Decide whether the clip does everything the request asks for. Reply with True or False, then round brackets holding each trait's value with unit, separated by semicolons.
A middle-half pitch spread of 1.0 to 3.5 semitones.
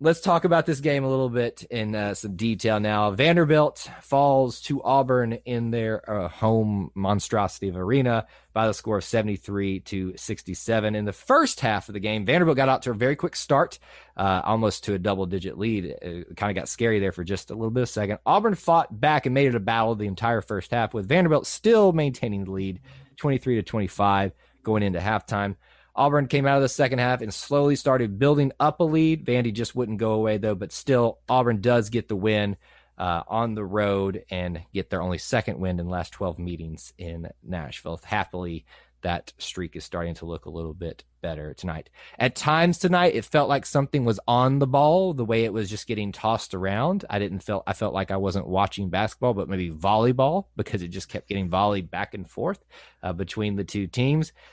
False (5.2 semitones)